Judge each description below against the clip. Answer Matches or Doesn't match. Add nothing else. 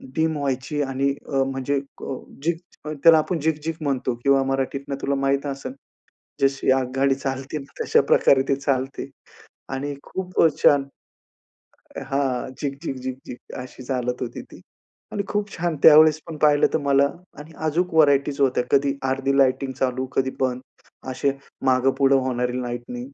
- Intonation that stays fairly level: Matches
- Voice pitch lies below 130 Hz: Doesn't match